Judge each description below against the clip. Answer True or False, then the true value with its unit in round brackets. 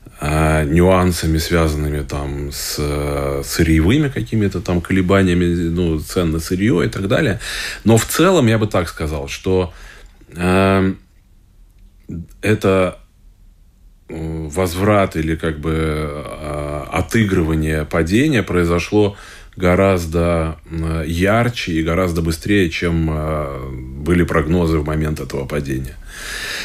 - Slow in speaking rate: True (100 wpm)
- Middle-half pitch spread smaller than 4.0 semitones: True (3.3 semitones)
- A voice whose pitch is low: True (85 Hz)